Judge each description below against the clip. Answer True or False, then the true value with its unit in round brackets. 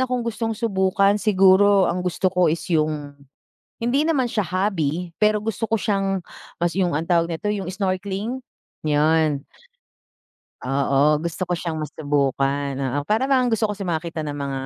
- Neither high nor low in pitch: True (180 Hz)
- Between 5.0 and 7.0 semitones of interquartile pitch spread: True (5.3 semitones)